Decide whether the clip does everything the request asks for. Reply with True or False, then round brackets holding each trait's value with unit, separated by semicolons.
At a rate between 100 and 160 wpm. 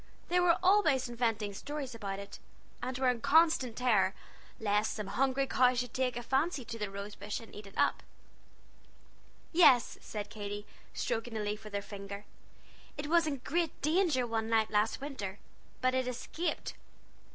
False (170 wpm)